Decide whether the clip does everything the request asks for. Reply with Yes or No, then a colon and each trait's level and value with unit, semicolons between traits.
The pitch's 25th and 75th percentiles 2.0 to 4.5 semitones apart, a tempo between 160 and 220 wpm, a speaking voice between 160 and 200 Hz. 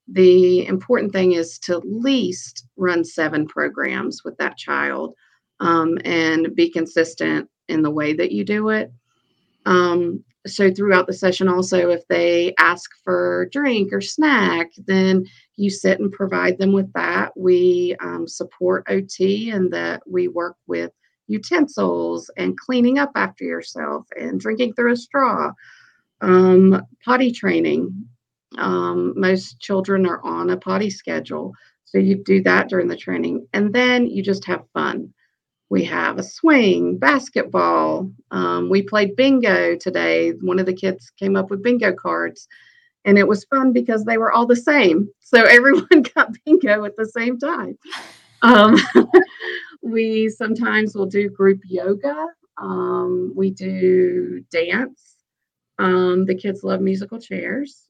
No: average, 4.2 semitones; average, 145 wpm; high, 190 Hz